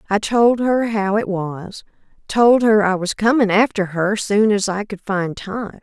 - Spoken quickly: No, average, 195 wpm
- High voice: Yes, high, 205 Hz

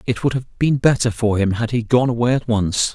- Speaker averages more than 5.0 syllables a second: Yes, 5.5 syllables/s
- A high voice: No, low, 120 Hz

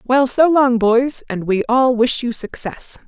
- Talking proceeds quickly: No, average, 195 wpm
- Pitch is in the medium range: No, high, 245 Hz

